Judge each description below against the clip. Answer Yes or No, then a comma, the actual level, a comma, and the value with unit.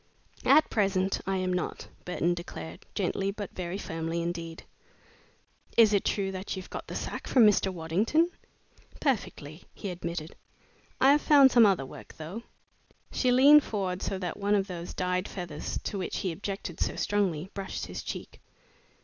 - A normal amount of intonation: Yes, average, 3.1 semitones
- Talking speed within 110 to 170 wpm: Yes, average, 165 wpm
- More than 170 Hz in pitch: Yes, high, 190 Hz